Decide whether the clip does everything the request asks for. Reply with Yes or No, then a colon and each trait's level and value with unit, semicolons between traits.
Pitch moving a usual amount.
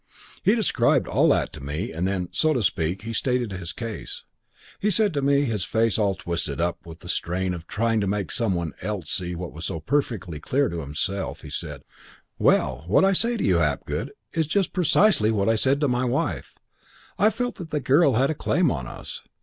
No: wide, 8.3 semitones